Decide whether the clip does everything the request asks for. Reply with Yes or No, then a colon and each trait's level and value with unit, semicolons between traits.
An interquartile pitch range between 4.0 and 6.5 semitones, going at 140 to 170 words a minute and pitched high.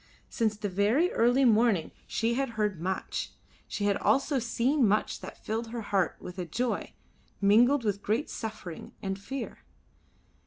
No: average, 3.3 semitones; average, 155 wpm; high, 220 Hz